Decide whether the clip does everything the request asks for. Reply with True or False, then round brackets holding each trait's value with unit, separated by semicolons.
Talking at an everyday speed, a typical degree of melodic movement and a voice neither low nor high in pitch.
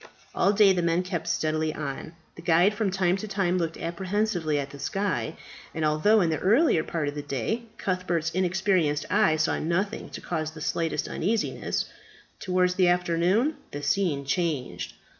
True (170 wpm; 3.6 semitones; 175 Hz)